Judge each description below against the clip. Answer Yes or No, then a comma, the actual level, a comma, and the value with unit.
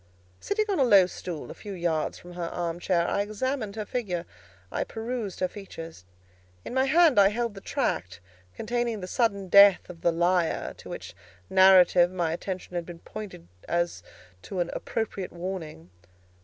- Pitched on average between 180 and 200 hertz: Yes, medium, 185 Hz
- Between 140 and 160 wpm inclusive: No, average, 170 wpm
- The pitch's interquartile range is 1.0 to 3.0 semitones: No, average, 3.8 semitones